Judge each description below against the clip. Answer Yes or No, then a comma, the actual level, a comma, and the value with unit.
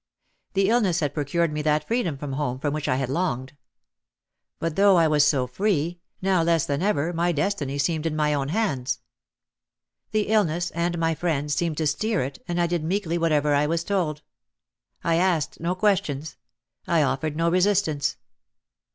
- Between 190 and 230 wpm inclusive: No, average, 175 wpm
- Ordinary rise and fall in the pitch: Yes, average, 3.2 semitones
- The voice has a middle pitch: Yes, medium, 165 Hz